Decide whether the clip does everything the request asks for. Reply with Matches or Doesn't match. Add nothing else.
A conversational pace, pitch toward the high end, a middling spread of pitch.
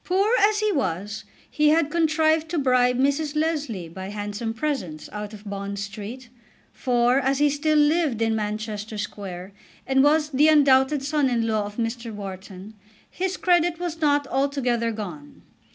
Doesn't match